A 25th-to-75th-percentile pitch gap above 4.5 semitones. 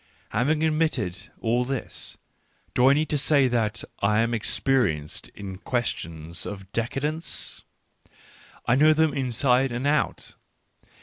Yes: average, 5.2 semitones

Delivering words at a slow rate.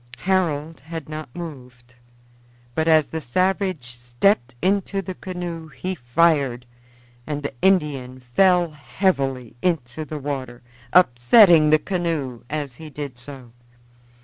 Yes: slow, 120 wpm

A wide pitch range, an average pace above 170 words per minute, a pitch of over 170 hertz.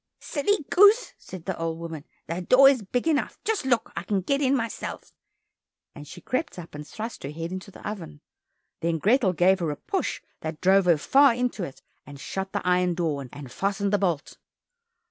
Yes: wide, 7.0 semitones; average, 200 wpm; medium, 185 Hz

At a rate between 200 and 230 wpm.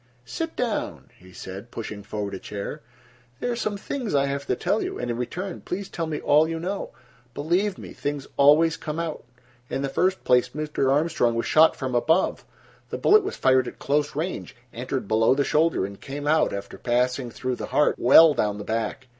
Yes: fast, 205 wpm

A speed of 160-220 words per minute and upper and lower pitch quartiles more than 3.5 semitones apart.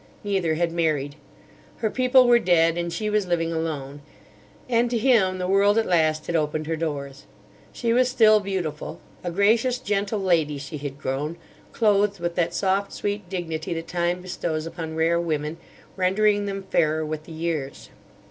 Yes: average, 170 wpm; average, 4.4 semitones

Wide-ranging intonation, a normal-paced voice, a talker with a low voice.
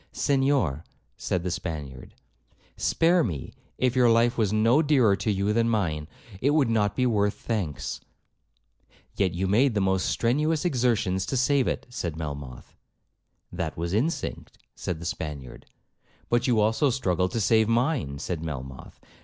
Yes: wide, 6.6 semitones; average, 155 wpm; low, 105 Hz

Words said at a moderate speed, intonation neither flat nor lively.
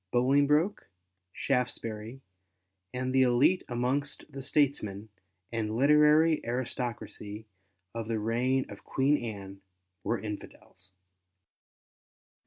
No: slow, 90 wpm; average, 4.0 semitones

